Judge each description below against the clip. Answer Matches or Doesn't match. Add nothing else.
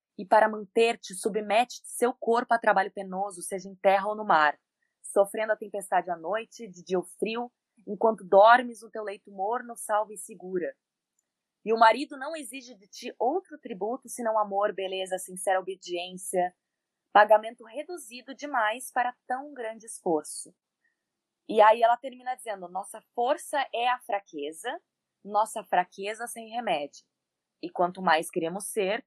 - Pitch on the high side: Matches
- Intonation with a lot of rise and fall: Doesn't match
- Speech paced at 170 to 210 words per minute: Doesn't match